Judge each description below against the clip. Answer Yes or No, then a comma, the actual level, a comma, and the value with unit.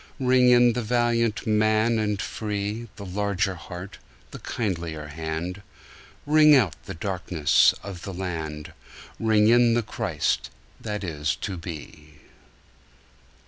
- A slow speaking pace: Yes, slow, 125 wpm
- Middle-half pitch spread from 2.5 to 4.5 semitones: No, average, 5.0 semitones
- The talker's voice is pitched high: No, low, 100 Hz